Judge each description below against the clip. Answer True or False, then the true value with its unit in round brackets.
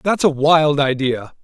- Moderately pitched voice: True (145 Hz)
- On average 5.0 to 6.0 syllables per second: False (3.9 syllables/s)